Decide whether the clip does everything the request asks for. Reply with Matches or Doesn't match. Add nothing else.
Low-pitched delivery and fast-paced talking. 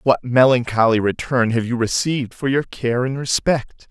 Doesn't match